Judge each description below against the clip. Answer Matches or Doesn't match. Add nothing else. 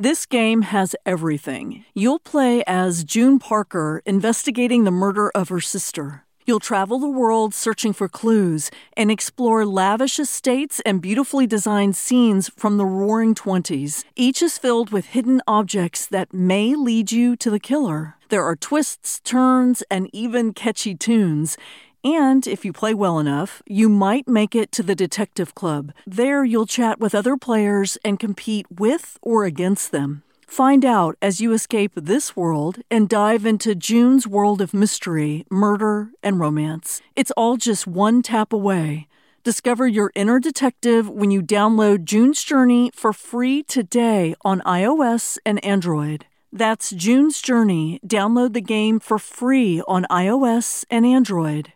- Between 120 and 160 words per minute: Matches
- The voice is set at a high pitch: Matches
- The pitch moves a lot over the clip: Doesn't match